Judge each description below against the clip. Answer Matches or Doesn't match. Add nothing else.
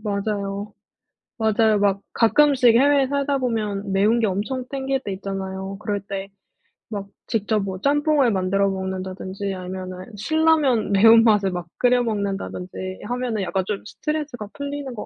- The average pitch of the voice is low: Doesn't match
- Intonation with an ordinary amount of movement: Matches